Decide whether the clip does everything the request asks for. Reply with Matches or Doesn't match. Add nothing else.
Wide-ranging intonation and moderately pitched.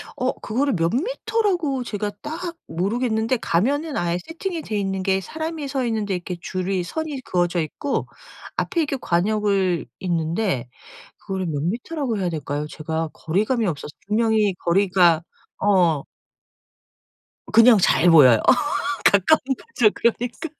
Doesn't match